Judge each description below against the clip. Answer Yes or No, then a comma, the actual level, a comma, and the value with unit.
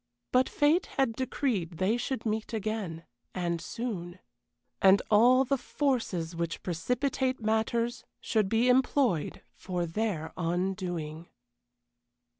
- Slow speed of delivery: Yes, slow, 110 wpm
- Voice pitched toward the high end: Yes, high, 215 Hz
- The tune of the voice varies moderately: No, wide, 6.1 semitones